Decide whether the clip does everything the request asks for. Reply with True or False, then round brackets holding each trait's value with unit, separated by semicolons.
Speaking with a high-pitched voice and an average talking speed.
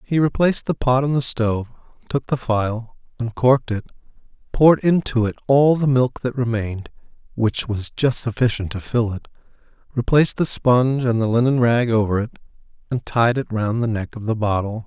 False (120 Hz; 180 wpm)